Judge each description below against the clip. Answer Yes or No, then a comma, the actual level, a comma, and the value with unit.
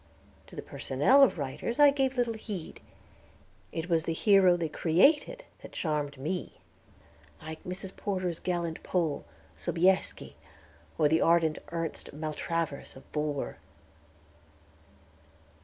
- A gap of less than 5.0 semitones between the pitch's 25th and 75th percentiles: Yes, average, 3.7 semitones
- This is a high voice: No, medium, 170 Hz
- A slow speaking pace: Yes, slow, 120 wpm